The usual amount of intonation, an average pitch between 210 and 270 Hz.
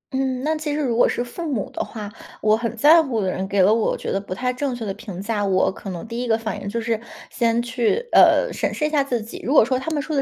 Yes: average, 4.1 semitones; high, 235 Hz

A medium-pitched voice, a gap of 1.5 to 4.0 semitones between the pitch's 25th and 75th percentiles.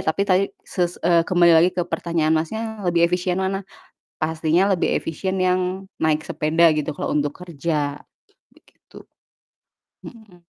Yes: medium, 175 Hz; narrow, 2.6 semitones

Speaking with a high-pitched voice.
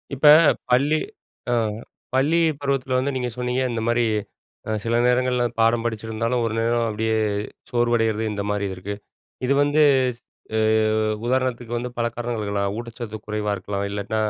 No: low, 120 Hz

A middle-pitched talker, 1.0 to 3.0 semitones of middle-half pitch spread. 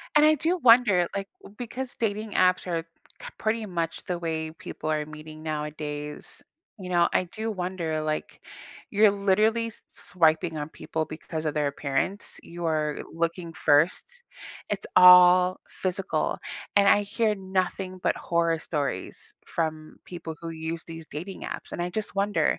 No: medium, 175 Hz; average, 4.1 semitones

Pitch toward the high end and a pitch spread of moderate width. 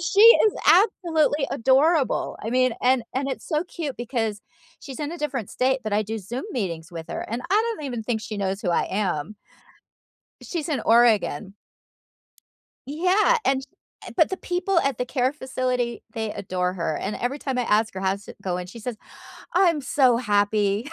No: very high, 250 Hz; wide, 6.0 semitones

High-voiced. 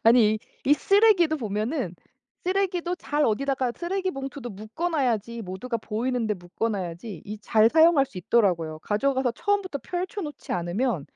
Yes: high, 245 Hz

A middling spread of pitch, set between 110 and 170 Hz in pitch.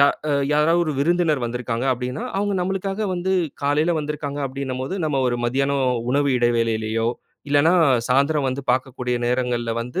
Yes: average, 3.7 semitones; medium, 140 Hz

